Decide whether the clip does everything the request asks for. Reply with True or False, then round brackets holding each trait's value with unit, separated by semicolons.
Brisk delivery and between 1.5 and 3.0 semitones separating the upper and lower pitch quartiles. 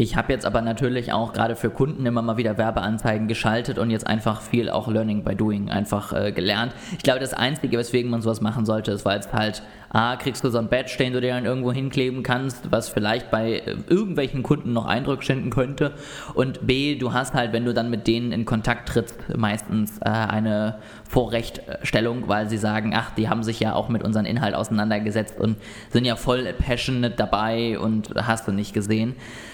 True (205 wpm; 2.5 semitones)